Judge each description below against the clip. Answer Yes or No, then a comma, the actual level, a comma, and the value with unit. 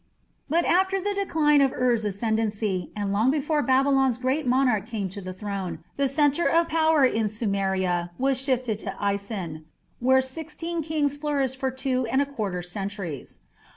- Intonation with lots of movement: Yes, wide, 6.1 semitones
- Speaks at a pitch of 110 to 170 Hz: No, very high, 255 Hz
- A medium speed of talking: Yes, average, 160 wpm